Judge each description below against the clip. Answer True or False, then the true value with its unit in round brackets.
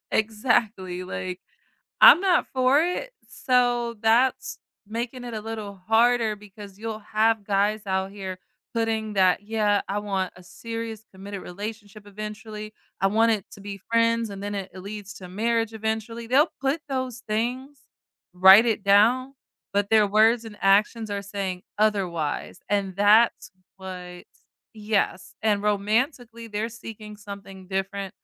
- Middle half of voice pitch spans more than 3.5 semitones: False (2.5 semitones)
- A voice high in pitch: True (215 Hz)